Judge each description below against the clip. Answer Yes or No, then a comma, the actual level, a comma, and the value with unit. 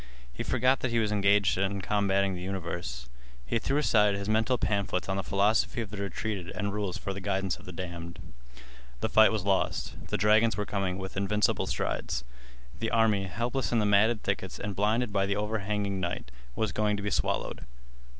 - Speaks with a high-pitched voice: No, low, 100 Hz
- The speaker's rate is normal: Yes, average, 195 wpm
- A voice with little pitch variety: Yes, narrow, 2.0 semitones